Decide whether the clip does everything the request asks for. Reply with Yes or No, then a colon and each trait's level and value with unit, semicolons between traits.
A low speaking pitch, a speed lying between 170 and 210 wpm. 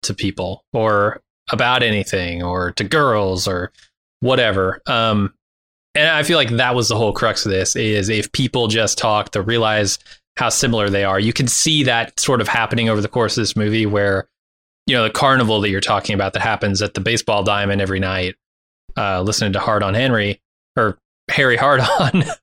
Yes: low, 105 Hz; average, 195 wpm